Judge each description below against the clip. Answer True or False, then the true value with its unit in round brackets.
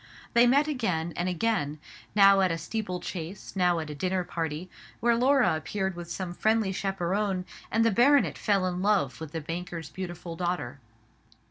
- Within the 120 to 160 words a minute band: False (170 wpm)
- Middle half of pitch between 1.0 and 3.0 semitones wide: False (3.8 semitones)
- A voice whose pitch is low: False (185 Hz)